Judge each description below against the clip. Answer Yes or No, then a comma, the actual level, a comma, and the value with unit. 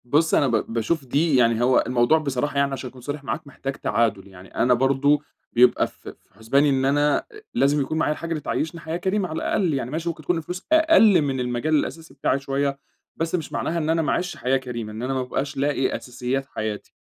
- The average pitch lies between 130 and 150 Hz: Yes, medium, 140 Hz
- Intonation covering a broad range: No, average, 3.8 semitones